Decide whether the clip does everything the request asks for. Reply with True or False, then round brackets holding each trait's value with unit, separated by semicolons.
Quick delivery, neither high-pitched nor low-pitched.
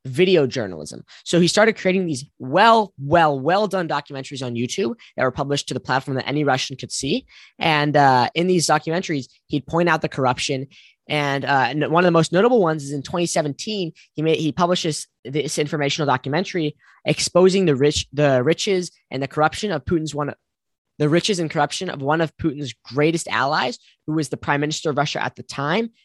False (195 wpm; 150 Hz)